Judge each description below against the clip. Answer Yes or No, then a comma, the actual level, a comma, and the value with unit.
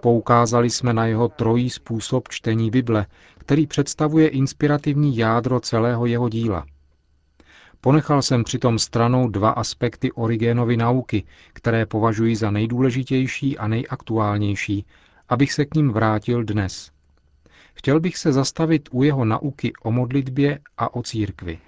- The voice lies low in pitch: Yes, low, 120 Hz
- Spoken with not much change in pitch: No, average, 3.3 semitones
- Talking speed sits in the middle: Yes, average, 130 wpm